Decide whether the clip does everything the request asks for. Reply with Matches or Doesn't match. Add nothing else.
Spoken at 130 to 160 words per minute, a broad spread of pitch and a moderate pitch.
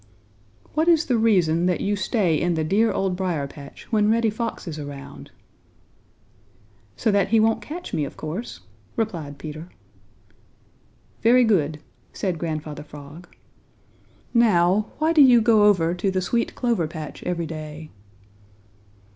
Matches